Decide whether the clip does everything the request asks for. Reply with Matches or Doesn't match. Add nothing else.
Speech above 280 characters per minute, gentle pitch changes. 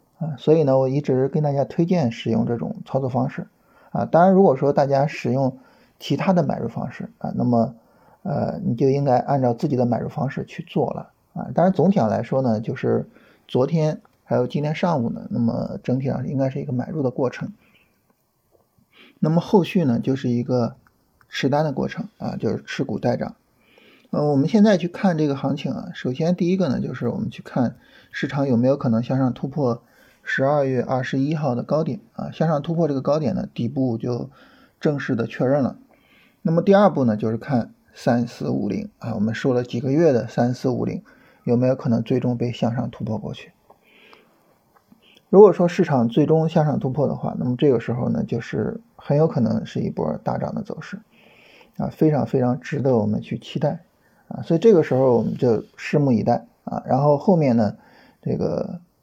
Doesn't match